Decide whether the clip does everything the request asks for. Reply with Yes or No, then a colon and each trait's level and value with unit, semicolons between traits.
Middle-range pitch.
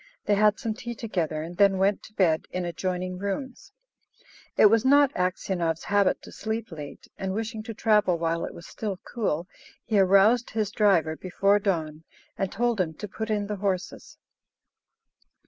No: high, 200 Hz